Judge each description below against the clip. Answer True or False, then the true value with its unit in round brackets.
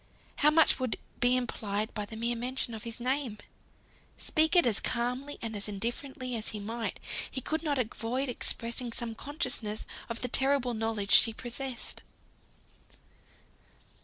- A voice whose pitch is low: False (240 Hz)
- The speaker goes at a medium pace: True (150 wpm)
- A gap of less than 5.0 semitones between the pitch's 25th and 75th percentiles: True (2.8 semitones)